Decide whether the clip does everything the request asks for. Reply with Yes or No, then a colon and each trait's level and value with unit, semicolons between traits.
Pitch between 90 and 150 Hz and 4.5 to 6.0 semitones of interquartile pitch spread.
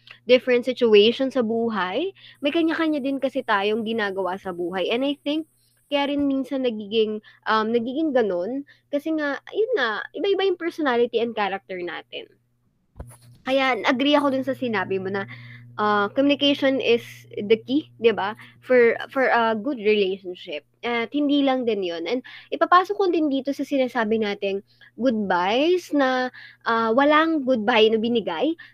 No: high, 245 Hz; wide, 5.4 semitones